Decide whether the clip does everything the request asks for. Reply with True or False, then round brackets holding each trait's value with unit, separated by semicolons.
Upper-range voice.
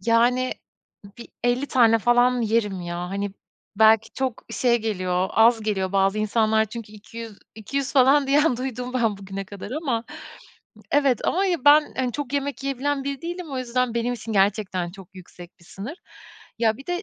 True (230 Hz)